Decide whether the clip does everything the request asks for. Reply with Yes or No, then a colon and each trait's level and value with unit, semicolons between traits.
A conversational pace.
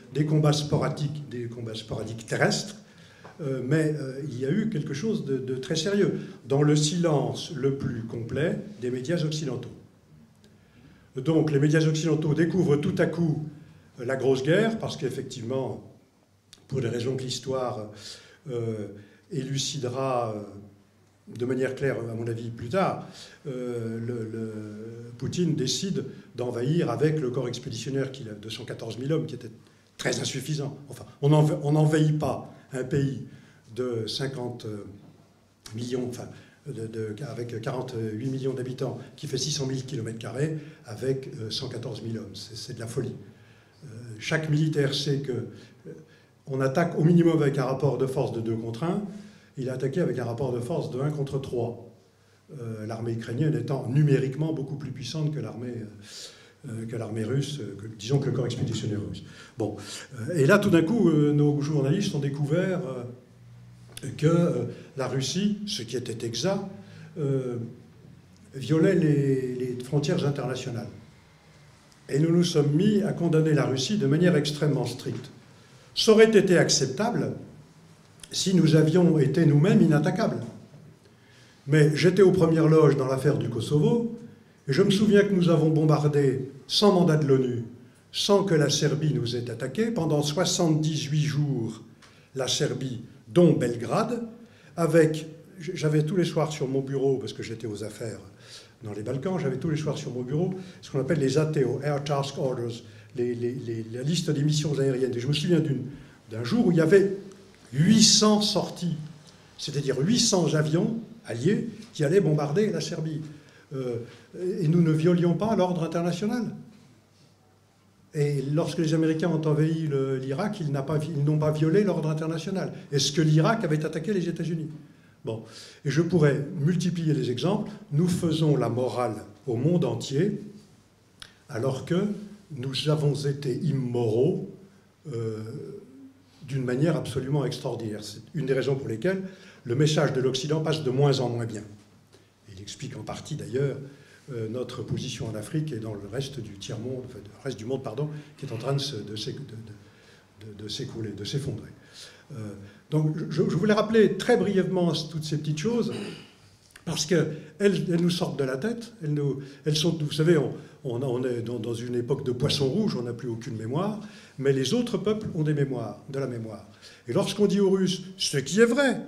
Yes: average, 170 wpm